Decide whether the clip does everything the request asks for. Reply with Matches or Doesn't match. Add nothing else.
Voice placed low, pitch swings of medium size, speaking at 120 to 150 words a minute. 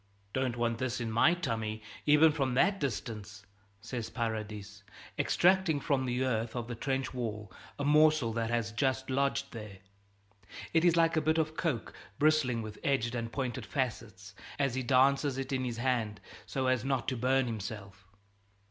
Doesn't match